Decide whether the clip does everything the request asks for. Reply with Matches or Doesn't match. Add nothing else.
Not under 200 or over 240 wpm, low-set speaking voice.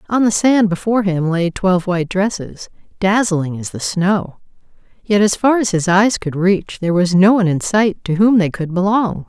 Doesn't match